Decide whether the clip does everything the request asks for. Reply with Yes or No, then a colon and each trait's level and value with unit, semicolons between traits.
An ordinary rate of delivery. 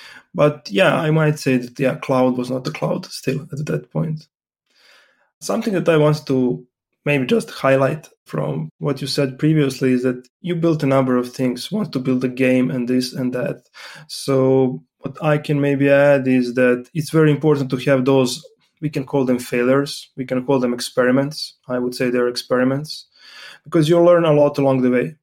Yes: average, 195 wpm